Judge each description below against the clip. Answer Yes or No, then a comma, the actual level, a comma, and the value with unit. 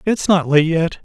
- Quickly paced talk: Yes, fast, 290 wpm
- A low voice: No, medium, 170 Hz